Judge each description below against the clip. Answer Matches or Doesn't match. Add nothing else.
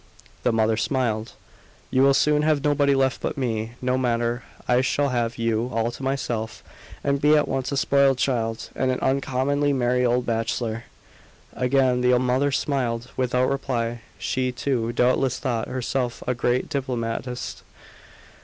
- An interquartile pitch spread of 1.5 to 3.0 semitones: Matches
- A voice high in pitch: Doesn't match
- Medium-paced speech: Matches